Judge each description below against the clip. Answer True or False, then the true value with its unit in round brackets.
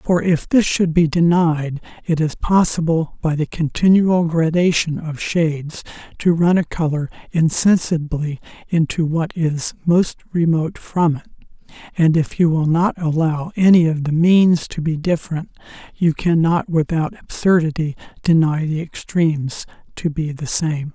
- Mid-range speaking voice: True (165 Hz)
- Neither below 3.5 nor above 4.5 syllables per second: True (4.4 syllables/s)